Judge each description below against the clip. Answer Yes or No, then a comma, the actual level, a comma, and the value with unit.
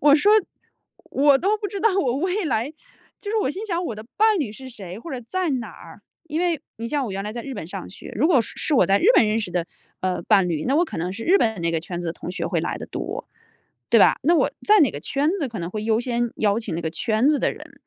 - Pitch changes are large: Yes, wide, 8.4 semitones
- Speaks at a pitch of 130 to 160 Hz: No, high, 240 Hz